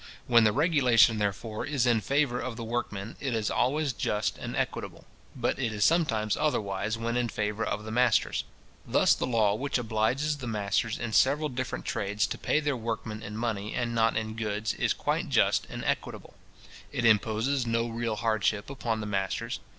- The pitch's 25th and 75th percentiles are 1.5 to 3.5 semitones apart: Yes, average, 2.8 semitones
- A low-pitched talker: Yes, low, 115 Hz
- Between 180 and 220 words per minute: Yes, average, 185 wpm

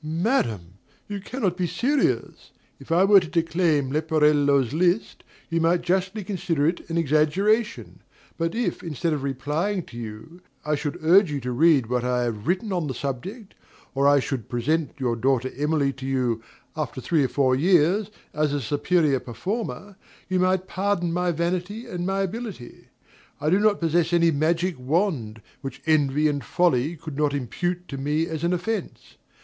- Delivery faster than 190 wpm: No, average, 175 wpm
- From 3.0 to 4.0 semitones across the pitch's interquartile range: No, average, 4.7 semitones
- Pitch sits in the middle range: Yes, medium, 160 Hz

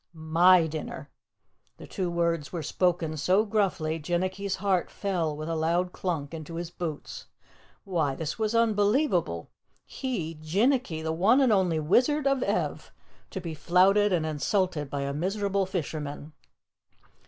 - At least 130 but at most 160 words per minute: Yes, average, 140 wpm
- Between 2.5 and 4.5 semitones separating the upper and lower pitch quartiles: Yes, average, 4.0 semitones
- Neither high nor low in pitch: Yes, medium, 175 Hz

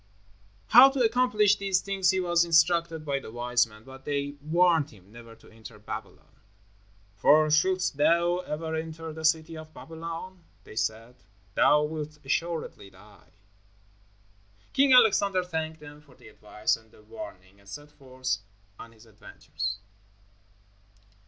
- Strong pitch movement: Yes, wide, 6.5 semitones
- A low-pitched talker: No, medium, 155 Hz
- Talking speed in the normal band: Yes, average, 145 wpm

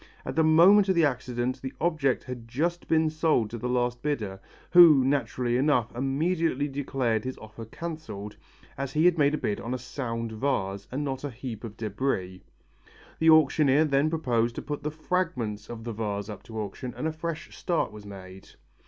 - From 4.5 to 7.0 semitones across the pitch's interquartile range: Yes, average, 5.3 semitones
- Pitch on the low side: Yes, low, 130 Hz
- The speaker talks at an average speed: Yes, average, 190 wpm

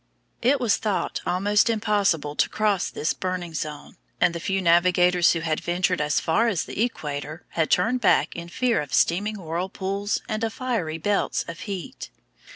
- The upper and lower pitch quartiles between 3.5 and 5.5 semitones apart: Yes, average, 4.1 semitones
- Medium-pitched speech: Yes, medium, 180 Hz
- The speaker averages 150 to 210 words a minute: Yes, average, 170 wpm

